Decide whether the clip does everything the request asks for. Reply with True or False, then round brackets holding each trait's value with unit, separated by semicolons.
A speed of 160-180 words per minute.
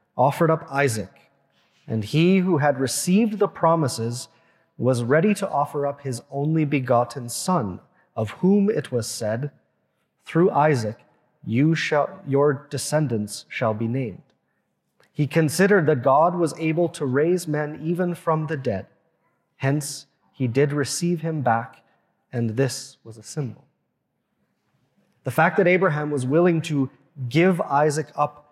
False (140 wpm)